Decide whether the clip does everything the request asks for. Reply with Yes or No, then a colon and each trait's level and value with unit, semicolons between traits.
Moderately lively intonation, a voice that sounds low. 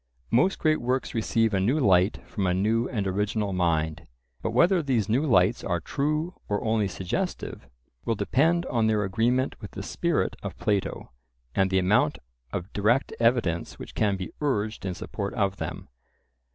Yes: average, 4.4 semitones; low, 105 Hz